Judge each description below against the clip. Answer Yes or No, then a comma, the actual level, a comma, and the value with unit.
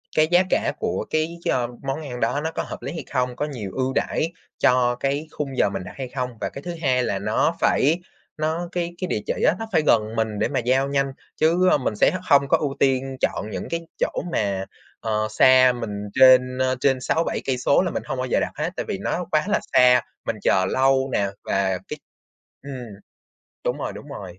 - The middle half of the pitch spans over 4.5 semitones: No, average, 3.9 semitones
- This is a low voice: Yes, low, 130 Hz